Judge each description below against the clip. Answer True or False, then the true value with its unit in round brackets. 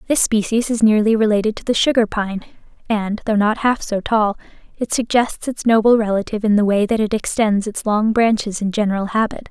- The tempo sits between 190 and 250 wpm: True (200 wpm)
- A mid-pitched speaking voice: False (215 Hz)